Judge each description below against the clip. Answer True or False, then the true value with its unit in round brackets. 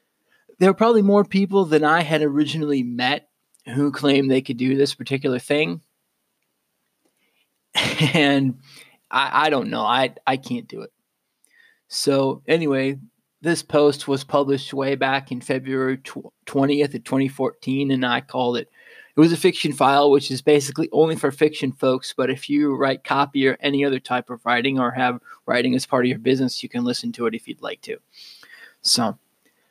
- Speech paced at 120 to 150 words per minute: False (175 wpm)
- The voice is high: False (140 Hz)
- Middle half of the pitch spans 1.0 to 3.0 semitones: True (2.4 semitones)